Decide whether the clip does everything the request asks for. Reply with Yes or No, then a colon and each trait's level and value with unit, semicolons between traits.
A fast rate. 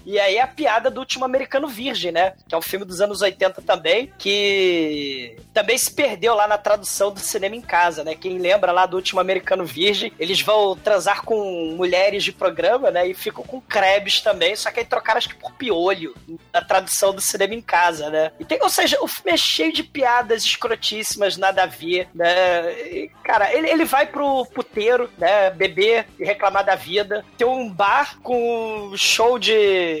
Yes: fast, 190 wpm